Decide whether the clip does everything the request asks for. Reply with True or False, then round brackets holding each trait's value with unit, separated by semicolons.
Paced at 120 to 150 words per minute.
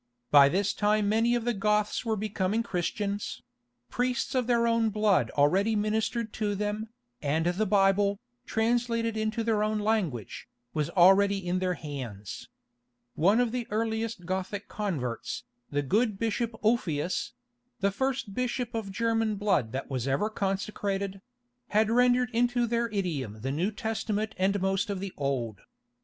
True (145 wpm)